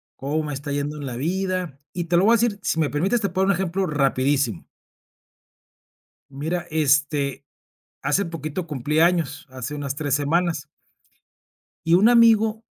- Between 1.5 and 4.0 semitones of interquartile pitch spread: No, average, 4.4 semitones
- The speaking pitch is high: No, medium, 155 Hz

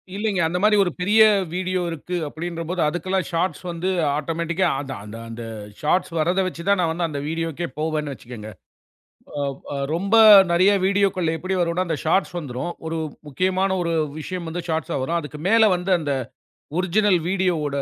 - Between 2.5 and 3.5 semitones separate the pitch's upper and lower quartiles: Yes, average, 2.8 semitones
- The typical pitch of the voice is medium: Yes, medium, 170 Hz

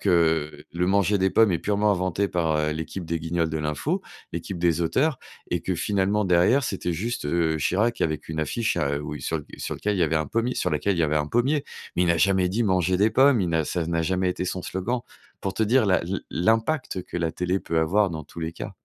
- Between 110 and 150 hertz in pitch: No, very low, 90 Hz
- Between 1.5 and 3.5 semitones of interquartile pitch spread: No, average, 4.0 semitones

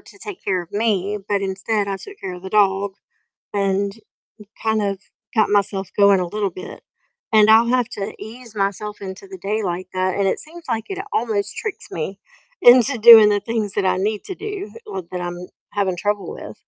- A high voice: Yes, high, 205 Hz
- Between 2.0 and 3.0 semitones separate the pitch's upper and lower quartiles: Yes, average, 2.7 semitones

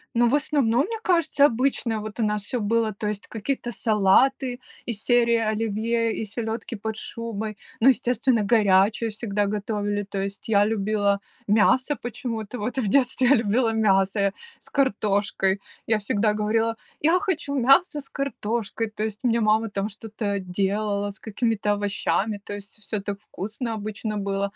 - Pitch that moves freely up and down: No, narrow, 2.6 semitones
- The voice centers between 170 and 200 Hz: No, high, 220 Hz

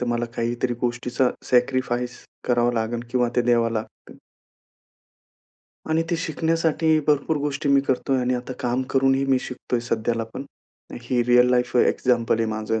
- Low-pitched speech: Yes, low, 125 Hz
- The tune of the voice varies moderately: No, narrow, 2.1 semitones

